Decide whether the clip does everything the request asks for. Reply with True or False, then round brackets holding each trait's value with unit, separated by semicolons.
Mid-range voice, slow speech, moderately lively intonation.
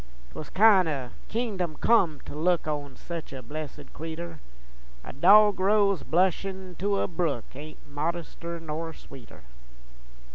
True (165 Hz; 130 wpm; 4.0 semitones)